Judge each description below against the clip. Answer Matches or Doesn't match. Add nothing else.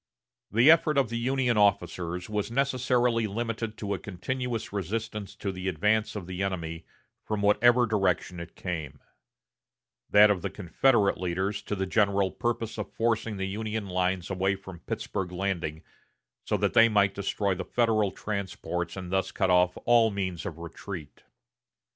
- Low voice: Matches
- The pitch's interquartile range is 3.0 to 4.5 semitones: Matches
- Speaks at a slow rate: Doesn't match